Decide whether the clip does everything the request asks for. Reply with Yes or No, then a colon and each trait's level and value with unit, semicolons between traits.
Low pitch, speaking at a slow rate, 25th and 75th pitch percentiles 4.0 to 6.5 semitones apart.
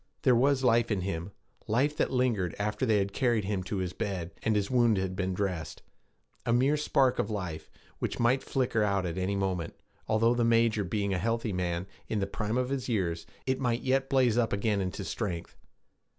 No: low, 105 Hz; average, 200 wpm; average, 4.3 semitones